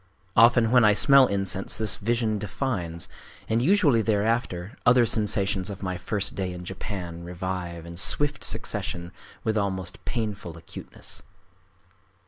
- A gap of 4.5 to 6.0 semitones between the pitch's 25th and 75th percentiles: No, average, 4.1 semitones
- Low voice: Yes, low, 100 Hz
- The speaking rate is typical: No, slow, 130 wpm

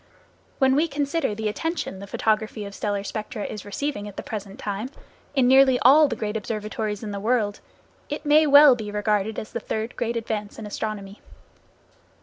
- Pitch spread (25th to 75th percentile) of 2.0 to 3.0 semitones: No, average, 4.1 semitones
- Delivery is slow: No, average, 180 wpm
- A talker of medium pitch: No, high, 220 Hz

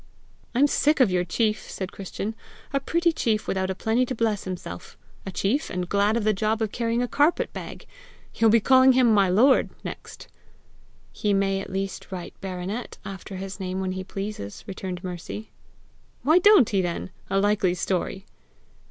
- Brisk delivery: No, average, 180 wpm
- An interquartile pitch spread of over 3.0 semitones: Yes, average, 3.6 semitones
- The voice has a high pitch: Yes, high, 200 Hz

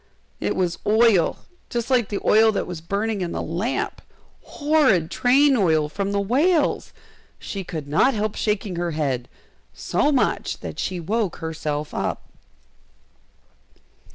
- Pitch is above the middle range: Yes, high, 200 Hz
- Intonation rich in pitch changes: Yes, wide, 5.9 semitones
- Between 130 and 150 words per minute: Yes, average, 140 wpm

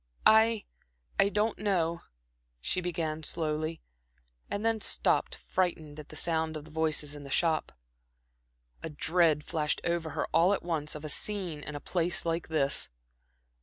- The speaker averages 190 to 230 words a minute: No, average, 155 wpm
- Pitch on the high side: No, medium, 160 Hz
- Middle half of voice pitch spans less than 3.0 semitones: Yes, narrow, 2.6 semitones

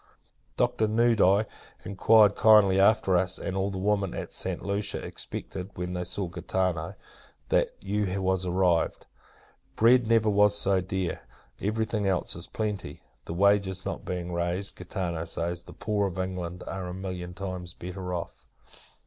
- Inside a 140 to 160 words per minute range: Yes, average, 155 wpm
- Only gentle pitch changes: Yes, narrow, 2.3 semitones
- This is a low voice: Yes, very low, 95 Hz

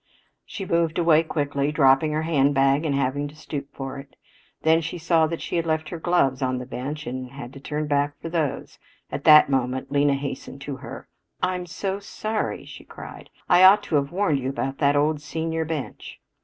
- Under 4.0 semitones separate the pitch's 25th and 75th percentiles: Yes, average, 2.9 semitones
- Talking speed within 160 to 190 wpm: No, fast, 205 wpm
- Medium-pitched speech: Yes, medium, 150 Hz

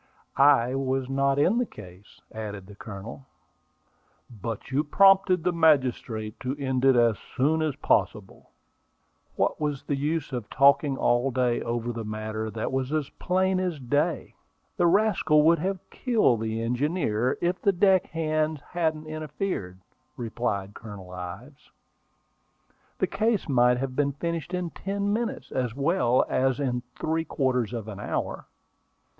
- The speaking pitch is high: No, low, 135 Hz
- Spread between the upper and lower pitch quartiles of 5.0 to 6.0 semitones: Yes, wide, 5.6 semitones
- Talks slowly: No, average, 150 wpm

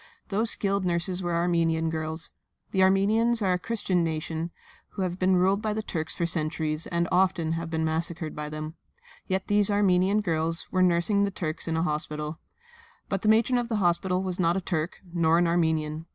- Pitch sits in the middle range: Yes, medium, 175 Hz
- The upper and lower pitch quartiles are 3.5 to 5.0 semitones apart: No, average, 3.1 semitones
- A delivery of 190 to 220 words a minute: Yes, average, 195 wpm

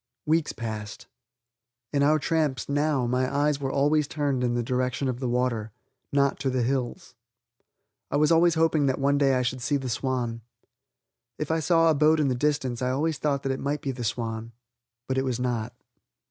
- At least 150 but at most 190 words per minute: No, average, 200 wpm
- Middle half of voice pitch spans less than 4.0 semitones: Yes, average, 2.9 semitones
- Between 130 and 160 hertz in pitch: Yes, low, 135 Hz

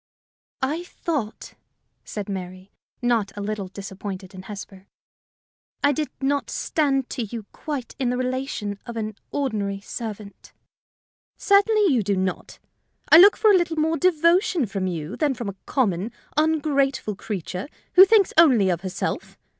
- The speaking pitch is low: No, high, 235 Hz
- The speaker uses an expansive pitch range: Yes, wide, 7.5 semitones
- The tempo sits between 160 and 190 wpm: No, average, 145 wpm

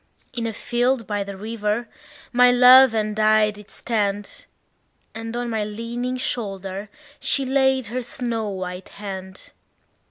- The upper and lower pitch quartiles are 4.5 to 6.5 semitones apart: No, average, 2.9 semitones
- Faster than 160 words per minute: No, slow, 135 wpm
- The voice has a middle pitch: No, high, 225 Hz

